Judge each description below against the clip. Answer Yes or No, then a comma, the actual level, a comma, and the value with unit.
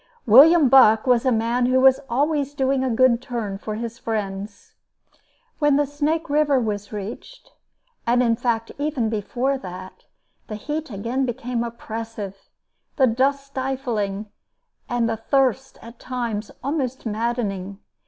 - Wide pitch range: No, average, 3.5 semitones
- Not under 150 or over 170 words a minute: No, slow, 135 wpm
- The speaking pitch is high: Yes, high, 240 Hz